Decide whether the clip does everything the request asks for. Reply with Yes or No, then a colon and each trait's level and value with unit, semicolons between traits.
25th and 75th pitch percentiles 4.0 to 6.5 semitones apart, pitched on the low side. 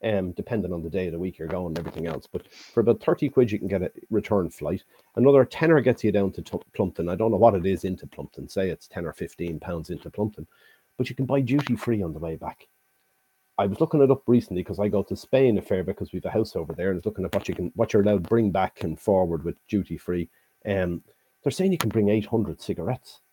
Yes: average, 4.7 semitones; low, 100 Hz